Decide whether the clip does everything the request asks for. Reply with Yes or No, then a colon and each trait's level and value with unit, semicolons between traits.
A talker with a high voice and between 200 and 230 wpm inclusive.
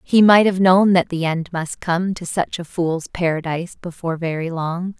No: medium, 175 Hz; fast, 205 wpm